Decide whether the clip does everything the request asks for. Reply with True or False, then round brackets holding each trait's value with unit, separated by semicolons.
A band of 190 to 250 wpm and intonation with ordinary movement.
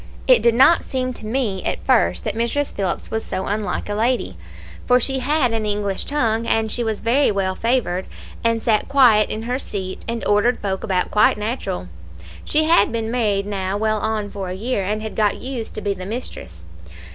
True (205 wpm; 3.4 semitones)